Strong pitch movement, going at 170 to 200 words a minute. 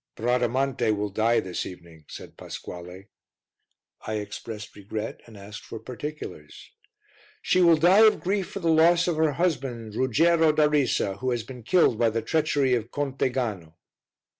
No: wide, 6.3 semitones; average, 160 wpm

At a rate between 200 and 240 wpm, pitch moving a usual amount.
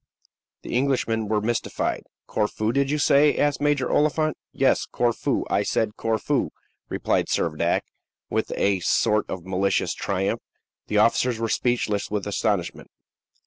No: slow, 135 wpm; average, 4.8 semitones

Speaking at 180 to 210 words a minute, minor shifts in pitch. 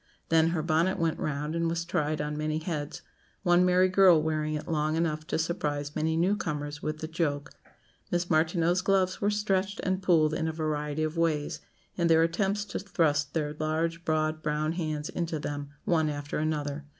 Yes: average, 185 wpm; narrow, 2.2 semitones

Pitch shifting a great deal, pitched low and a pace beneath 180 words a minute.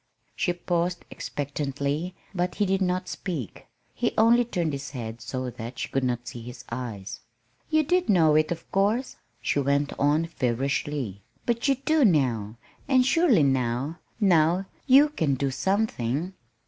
No: wide, 7.0 semitones; medium, 155 Hz; average, 160 wpm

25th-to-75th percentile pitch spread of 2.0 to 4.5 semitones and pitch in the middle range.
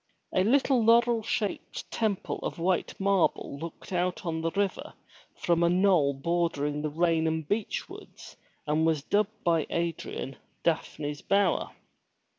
Yes: average, 3.8 semitones; medium, 170 Hz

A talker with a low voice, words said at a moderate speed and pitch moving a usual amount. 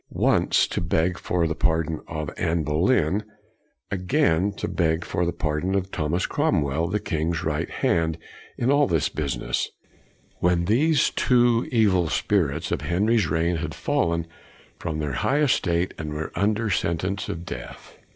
Yes: very low, 85 Hz; average, 150 wpm; average, 4.0 semitones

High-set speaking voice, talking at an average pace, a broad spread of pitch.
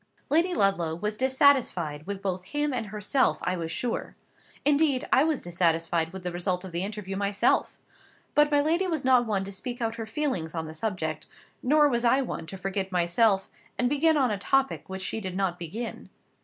Yes: high, 205 Hz; average, 195 wpm; wide, 6.5 semitones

